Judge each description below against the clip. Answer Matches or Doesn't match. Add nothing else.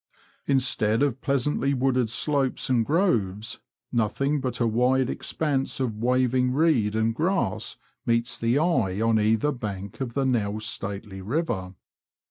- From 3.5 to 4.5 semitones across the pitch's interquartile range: Matches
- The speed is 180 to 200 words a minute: Doesn't match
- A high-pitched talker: Doesn't match